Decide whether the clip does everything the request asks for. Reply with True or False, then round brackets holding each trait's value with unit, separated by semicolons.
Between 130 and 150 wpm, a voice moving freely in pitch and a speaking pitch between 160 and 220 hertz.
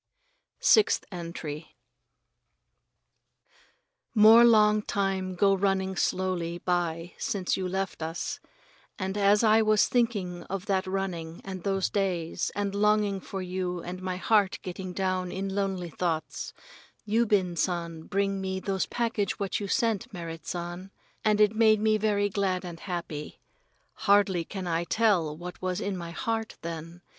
False (145 wpm; 2.6 semitones; 190 Hz)